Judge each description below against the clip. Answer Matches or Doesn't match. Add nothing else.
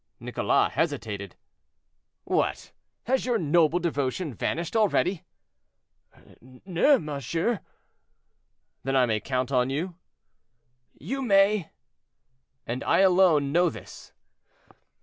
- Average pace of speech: Doesn't match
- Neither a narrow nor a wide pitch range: Doesn't match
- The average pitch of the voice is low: Doesn't match